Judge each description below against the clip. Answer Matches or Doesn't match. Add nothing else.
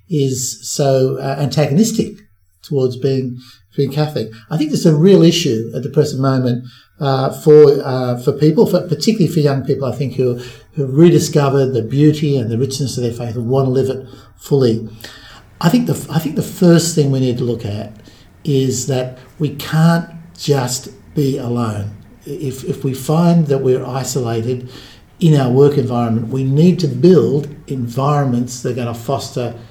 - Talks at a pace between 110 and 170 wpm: Doesn't match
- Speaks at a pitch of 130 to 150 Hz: Matches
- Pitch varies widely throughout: Doesn't match